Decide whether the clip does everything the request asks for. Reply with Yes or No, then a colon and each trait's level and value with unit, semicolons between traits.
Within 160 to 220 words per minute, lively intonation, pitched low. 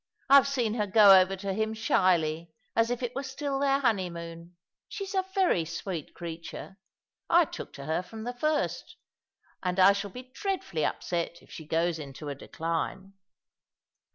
No: average, 165 wpm; wide, 6.8 semitones; high, 195 Hz